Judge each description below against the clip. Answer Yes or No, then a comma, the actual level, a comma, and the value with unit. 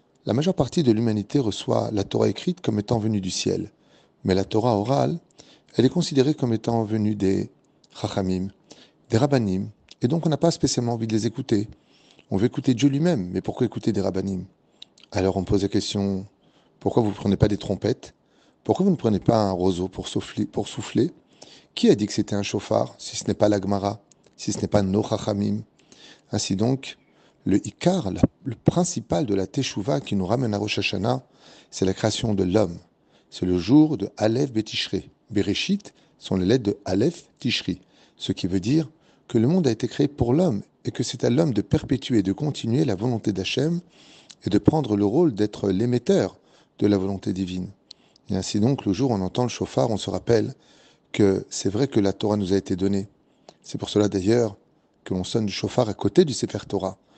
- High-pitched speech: No, low, 105 Hz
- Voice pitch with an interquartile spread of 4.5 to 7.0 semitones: No, average, 4.1 semitones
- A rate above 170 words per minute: Yes, average, 205 wpm